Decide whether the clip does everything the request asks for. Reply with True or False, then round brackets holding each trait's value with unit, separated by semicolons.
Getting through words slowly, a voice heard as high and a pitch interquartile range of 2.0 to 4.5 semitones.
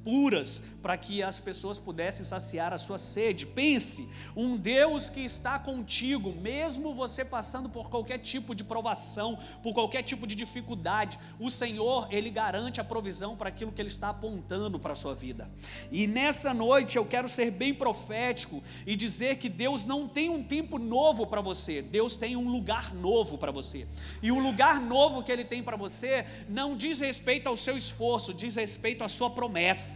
False (180 wpm; 240 Hz; 3.3 semitones)